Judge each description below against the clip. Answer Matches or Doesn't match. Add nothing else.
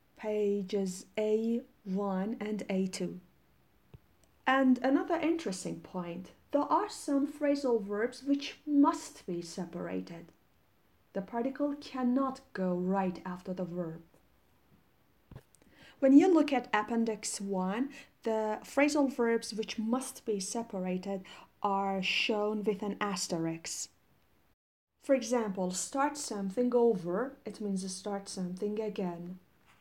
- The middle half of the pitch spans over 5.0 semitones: Matches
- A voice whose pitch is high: Matches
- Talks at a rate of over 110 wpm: Doesn't match